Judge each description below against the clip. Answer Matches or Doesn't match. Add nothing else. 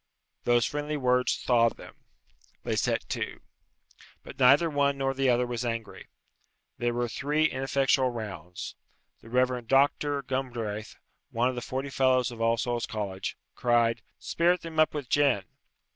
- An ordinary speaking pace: Matches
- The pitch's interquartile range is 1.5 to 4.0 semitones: Matches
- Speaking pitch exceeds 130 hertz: Doesn't match